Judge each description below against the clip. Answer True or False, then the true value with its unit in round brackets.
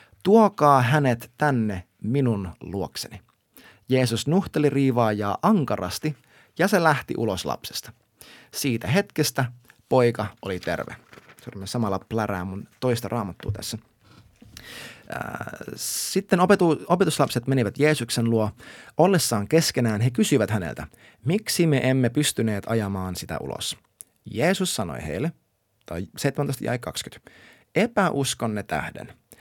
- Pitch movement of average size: False (5.8 semitones)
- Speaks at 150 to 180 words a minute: False (95 wpm)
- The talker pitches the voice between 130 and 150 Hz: False (120 Hz)